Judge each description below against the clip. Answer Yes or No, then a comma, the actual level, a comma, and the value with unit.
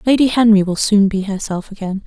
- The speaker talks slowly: No, fast, 205 wpm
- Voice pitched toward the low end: No, high, 205 Hz